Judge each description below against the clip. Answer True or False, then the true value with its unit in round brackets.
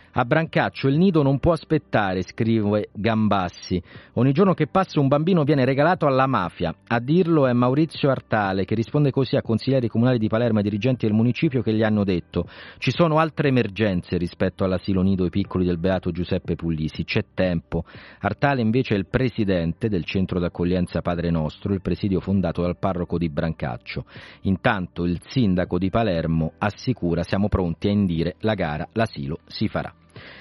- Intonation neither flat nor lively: False (6.3 semitones)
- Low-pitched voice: True (105 Hz)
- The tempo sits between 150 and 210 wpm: True (170 wpm)